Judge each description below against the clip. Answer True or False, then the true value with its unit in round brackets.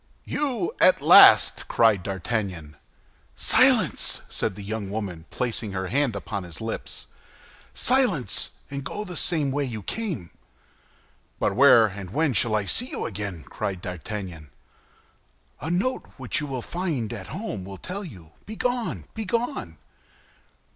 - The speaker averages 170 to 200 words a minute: False (140 wpm)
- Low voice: True (115 Hz)